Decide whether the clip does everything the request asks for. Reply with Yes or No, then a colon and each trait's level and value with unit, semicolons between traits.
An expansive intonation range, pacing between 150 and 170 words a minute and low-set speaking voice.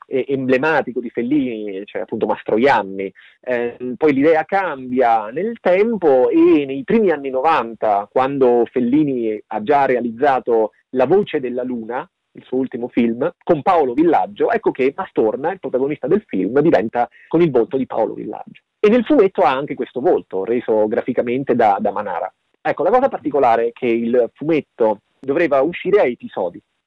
Yes: wide, 5.7 semitones; average, 160 wpm; low, 130 Hz